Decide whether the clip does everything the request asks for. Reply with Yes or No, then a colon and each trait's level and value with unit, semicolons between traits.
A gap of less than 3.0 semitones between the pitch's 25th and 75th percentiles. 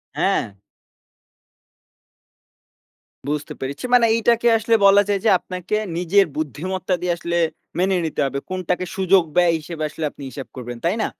No: average, 4.3 semitones